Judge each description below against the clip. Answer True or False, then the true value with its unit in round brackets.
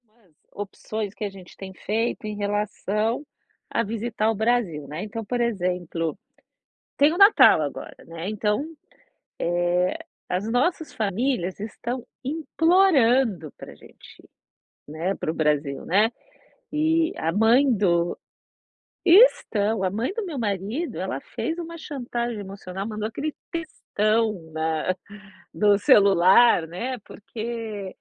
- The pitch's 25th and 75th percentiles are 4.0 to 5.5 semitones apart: True (4.7 semitones)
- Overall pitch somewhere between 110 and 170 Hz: False (215 Hz)